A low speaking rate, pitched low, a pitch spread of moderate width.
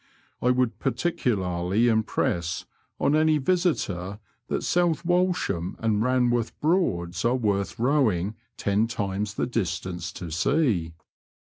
No: slow, 115 wpm; low, 110 Hz; wide, 6.4 semitones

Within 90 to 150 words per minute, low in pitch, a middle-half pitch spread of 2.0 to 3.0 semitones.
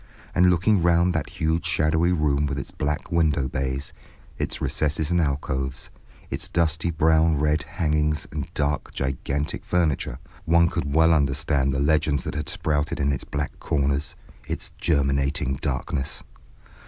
Yes: average, 145 wpm; very low, 75 Hz; average, 2.7 semitones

